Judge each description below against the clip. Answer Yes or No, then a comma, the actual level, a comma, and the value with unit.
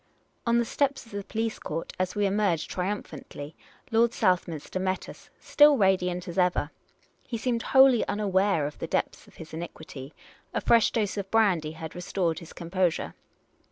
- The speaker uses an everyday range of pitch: Yes, average, 4.9 semitones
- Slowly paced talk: No, average, 175 wpm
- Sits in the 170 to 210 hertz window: Yes, high, 190 Hz